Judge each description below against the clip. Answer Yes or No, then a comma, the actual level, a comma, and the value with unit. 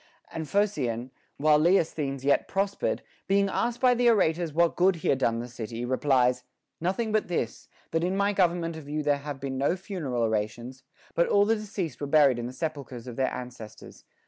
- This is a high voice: No, medium, 150 Hz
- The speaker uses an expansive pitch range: Yes, wide, 6.8 semitones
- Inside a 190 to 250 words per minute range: Yes, average, 195 wpm